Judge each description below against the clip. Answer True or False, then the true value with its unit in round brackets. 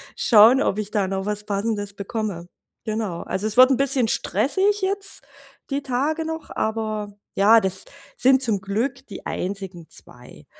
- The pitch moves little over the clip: False (4.9 semitones)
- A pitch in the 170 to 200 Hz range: False (220 Hz)